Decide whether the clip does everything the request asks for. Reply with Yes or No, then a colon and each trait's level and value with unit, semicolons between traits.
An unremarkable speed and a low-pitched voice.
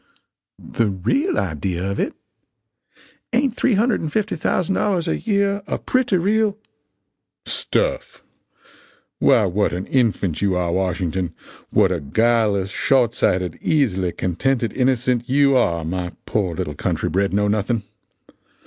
No: slow, 120 wpm; low, 115 Hz